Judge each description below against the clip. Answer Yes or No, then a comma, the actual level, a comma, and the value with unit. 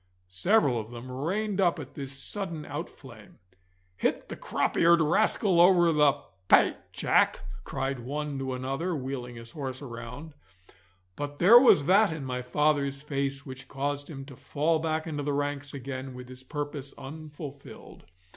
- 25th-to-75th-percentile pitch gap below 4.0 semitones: Yes, average, 3.3 semitones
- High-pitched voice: No, medium, 140 Hz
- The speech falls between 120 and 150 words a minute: No, average, 160 wpm